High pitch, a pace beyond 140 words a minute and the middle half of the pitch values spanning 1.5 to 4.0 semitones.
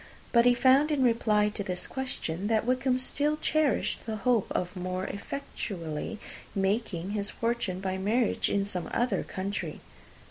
No: high, 215 Hz; average, 150 wpm; average, 4.6 semitones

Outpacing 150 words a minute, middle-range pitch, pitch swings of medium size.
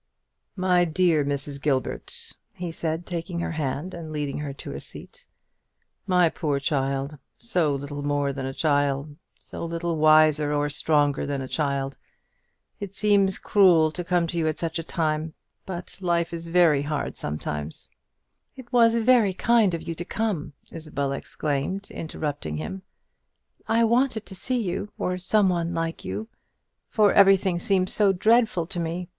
Yes: average, 160 wpm; medium, 165 Hz; average, 4.4 semitones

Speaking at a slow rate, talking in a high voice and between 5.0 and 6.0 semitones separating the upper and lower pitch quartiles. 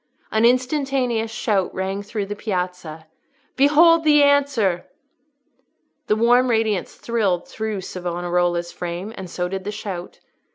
Yes: slow, 125 wpm; high, 210 Hz; average, 5.3 semitones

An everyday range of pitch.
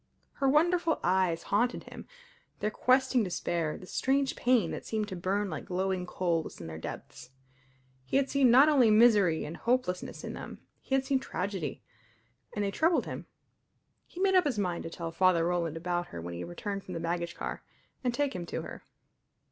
No: wide, 7.2 semitones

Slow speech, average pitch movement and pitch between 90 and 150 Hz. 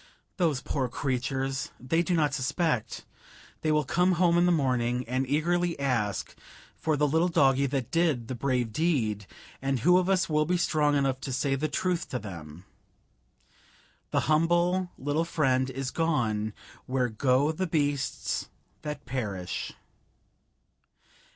No: average, 145 wpm; average, 4.4 semitones; medium, 140 Hz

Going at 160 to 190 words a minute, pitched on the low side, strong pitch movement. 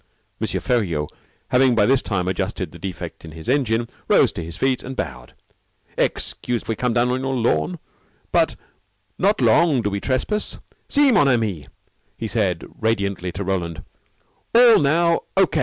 Yes: average, 165 wpm; low, 115 Hz; wide, 6.4 semitones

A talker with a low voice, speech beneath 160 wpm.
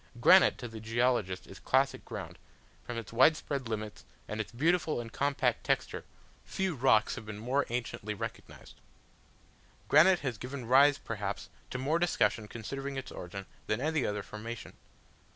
Yes: low, 120 Hz; average, 150 wpm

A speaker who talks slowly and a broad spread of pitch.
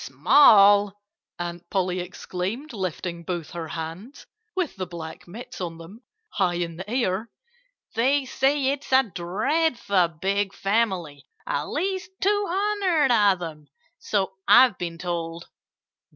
Yes: slow, 130 wpm; wide, 7.1 semitones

